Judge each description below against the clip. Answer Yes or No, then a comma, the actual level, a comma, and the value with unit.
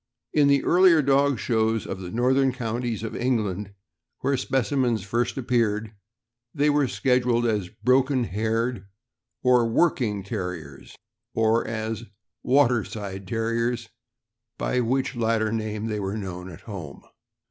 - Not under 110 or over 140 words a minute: Yes, slow, 135 wpm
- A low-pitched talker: Yes, low, 115 Hz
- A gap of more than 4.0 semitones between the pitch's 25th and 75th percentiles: No, average, 3.2 semitones